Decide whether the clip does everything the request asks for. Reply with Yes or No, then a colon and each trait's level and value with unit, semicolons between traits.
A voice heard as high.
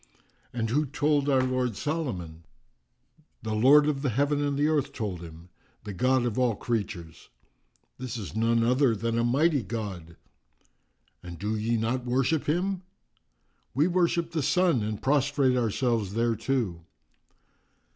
No: low, 125 Hz